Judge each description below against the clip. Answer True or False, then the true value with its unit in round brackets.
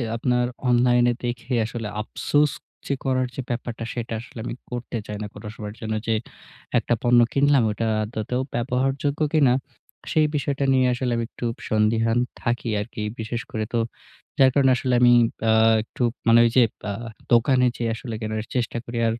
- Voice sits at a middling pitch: False (120 Hz)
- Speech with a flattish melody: True (2.1 semitones)